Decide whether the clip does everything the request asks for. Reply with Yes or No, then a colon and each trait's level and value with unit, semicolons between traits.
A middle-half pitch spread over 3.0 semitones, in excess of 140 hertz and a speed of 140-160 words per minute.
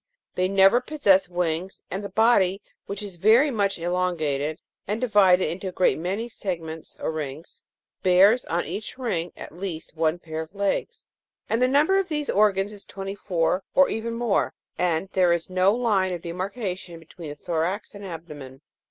No: average, 3.6 semitones; high, 190 Hz; average, 170 wpm